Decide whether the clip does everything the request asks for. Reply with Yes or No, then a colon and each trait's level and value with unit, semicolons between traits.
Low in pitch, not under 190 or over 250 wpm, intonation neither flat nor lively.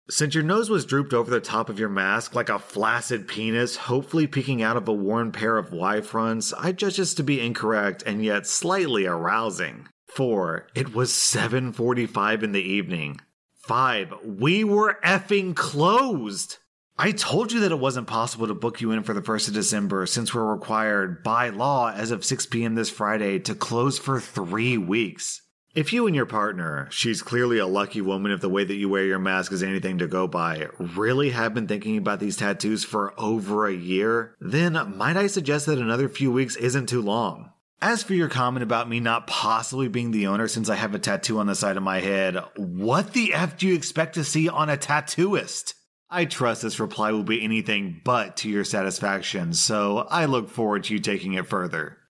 No: low, 115 Hz; fast, 205 wpm; wide, 5.9 semitones